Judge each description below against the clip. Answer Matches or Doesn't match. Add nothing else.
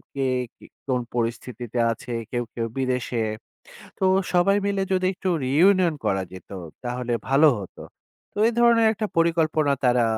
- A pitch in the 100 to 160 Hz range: Matches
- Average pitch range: Doesn't match